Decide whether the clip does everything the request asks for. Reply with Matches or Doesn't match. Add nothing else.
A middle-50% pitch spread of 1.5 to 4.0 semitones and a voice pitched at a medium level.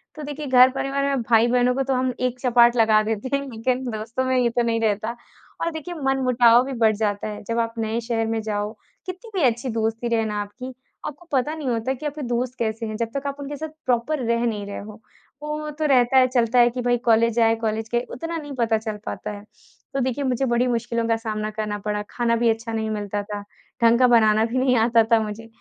Doesn't match